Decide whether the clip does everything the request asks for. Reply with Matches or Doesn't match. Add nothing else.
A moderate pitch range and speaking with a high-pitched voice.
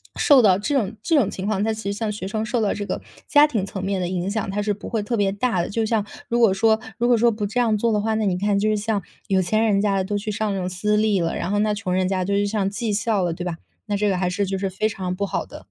Doesn't match